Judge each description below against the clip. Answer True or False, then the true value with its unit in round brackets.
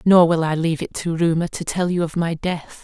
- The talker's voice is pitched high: False (170 Hz)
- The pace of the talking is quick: True (275 wpm)